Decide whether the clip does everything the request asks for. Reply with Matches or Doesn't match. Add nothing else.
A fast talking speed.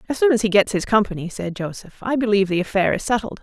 Matches